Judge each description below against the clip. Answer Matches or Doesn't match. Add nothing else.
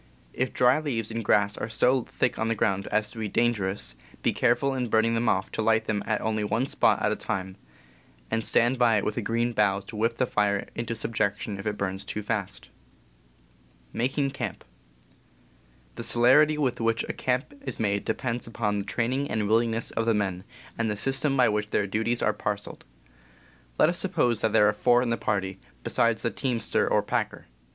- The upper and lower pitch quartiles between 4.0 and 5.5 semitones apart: Doesn't match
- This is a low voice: Matches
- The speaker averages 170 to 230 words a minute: Matches